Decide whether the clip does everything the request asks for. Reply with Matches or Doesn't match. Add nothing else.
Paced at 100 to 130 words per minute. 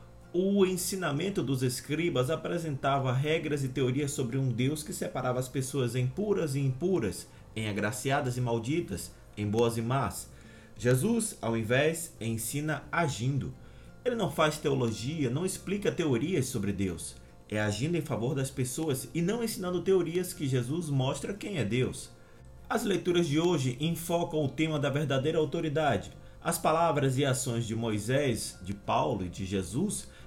Doesn't match